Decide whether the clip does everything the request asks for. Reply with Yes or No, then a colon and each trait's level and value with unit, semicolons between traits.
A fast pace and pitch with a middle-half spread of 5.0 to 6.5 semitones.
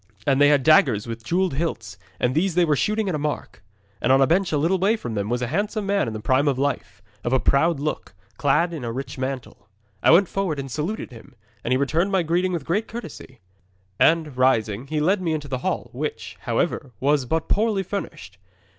Yes: fast, 225 wpm; wide, 5.5 semitones